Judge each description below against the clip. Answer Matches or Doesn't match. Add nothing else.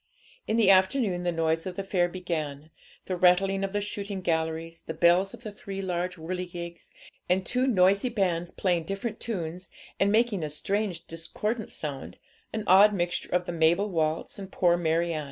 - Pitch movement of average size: Matches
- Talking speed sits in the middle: Matches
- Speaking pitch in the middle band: Matches